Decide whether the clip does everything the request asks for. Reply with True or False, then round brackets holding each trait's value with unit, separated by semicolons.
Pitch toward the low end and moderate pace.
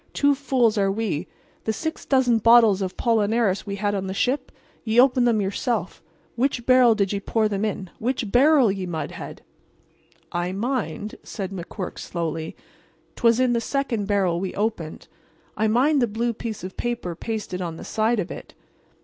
False (220 Hz; 165 wpm)